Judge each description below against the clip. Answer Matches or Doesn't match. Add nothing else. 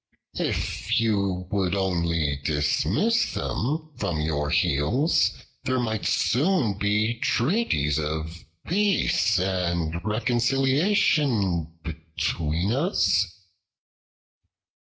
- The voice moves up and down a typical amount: Doesn't match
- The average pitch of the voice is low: Matches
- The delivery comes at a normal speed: Doesn't match